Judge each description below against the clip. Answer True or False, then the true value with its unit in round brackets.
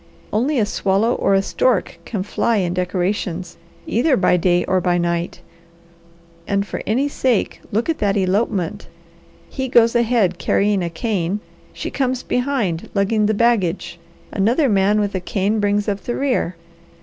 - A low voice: False (205 Hz)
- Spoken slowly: False (160 wpm)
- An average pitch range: True (4.2 semitones)